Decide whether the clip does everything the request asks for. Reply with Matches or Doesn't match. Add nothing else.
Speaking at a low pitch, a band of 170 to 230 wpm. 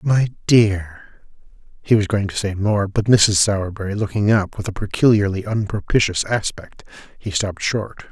Doesn't match